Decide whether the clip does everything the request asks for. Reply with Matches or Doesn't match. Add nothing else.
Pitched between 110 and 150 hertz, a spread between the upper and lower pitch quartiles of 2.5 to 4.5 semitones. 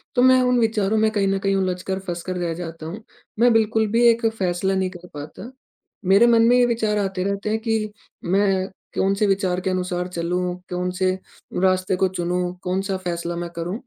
Doesn't match